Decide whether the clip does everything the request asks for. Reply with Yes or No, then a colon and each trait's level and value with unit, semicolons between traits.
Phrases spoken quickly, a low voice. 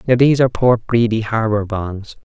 No: average, 185 wpm; low, 115 Hz